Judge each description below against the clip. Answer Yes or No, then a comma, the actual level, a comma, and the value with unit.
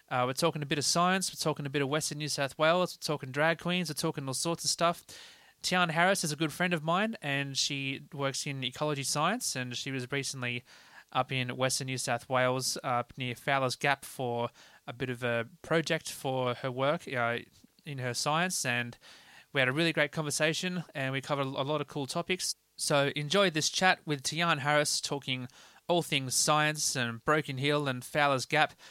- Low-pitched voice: No, medium, 145 Hz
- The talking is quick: Yes, fast, 210 wpm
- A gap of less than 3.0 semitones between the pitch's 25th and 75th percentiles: No, average, 3.7 semitones